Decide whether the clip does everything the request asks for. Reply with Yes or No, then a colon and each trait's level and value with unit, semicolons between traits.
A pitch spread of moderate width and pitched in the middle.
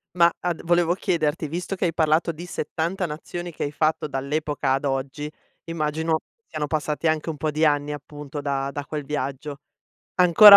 No: narrow, 2.3 semitones; medium, 155 Hz